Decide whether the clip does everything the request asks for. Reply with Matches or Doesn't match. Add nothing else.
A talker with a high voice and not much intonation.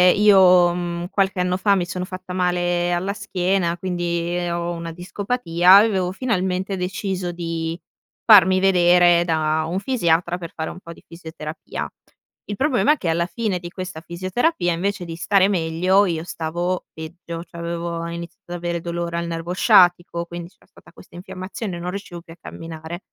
Doesn't match